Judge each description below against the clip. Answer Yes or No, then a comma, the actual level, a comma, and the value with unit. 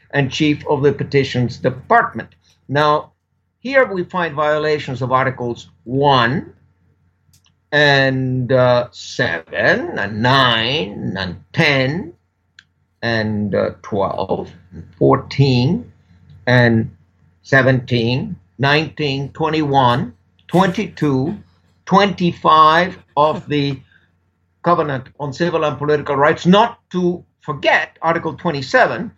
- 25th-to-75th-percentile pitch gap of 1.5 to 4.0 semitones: No, average, 4.4 semitones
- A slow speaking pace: Yes, slow, 95 wpm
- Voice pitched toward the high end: No, medium, 140 Hz